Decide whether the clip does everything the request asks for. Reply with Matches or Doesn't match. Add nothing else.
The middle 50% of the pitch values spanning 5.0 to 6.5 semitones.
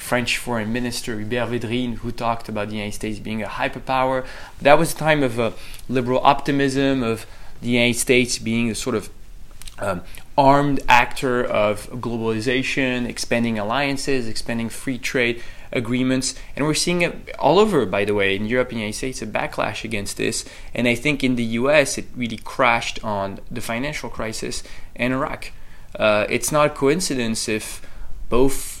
Doesn't match